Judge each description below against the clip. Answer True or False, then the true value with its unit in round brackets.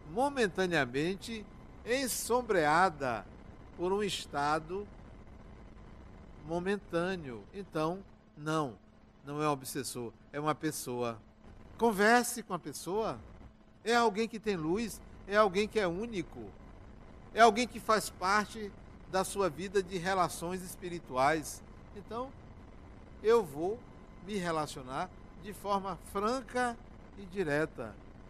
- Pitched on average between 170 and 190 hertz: True (185 Hz)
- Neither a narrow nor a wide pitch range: False (6.1 semitones)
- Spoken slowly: True (105 wpm)